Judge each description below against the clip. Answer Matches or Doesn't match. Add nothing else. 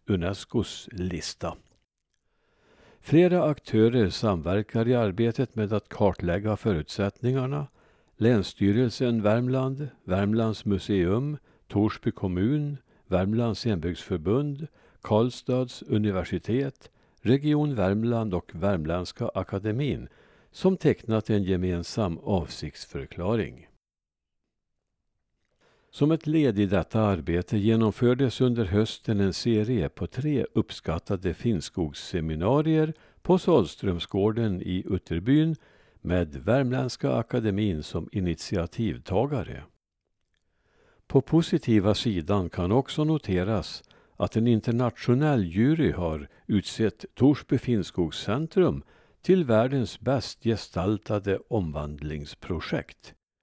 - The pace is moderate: Doesn't match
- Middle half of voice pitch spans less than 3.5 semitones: Doesn't match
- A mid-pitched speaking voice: Doesn't match